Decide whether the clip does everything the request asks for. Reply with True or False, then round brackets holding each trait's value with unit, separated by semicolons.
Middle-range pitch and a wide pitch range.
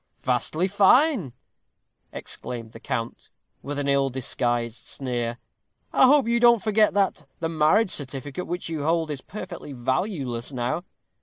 True (150 Hz; 7.3 semitones)